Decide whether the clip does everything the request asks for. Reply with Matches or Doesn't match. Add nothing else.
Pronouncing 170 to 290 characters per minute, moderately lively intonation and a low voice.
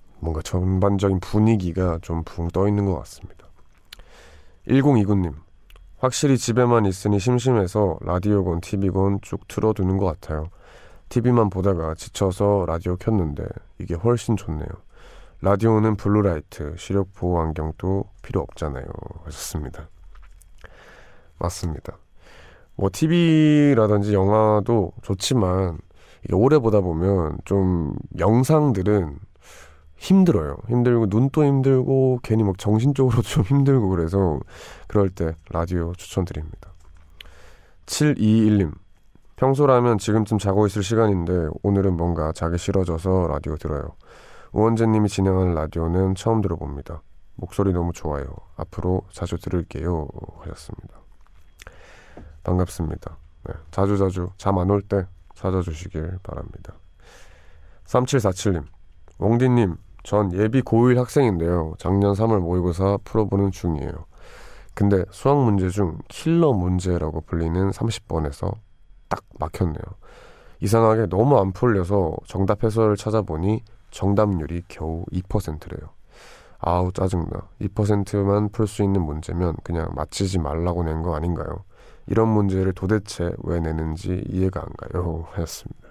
Matches